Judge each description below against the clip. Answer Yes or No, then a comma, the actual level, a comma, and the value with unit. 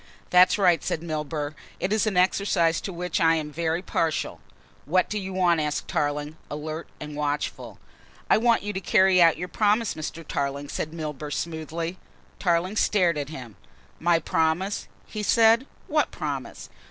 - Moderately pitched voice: Yes, medium, 170 Hz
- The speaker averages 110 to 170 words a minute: Yes, average, 165 wpm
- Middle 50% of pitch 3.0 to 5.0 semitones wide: Yes, average, 3.6 semitones